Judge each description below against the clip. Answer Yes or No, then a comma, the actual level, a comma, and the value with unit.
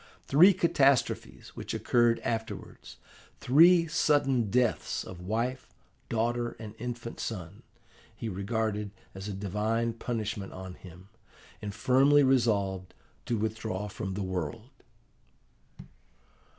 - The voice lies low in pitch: Yes, low, 110 Hz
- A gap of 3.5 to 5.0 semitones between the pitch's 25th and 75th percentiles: Yes, average, 3.9 semitones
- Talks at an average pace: No, slow, 110 wpm